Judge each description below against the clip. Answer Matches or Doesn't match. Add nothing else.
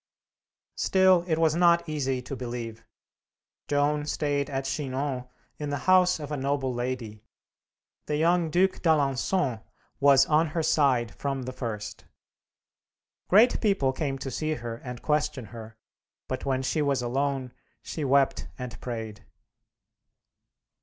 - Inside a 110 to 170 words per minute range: Matches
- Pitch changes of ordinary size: Matches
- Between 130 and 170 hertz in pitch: Matches